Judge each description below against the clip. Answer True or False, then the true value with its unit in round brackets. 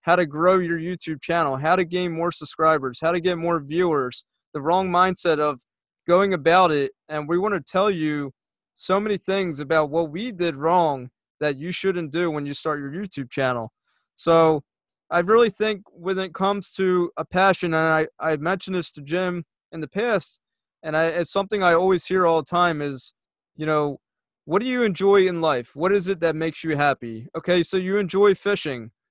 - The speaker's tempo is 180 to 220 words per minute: True (200 wpm)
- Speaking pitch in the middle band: True (170 Hz)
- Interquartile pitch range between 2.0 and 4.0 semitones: True (3.4 semitones)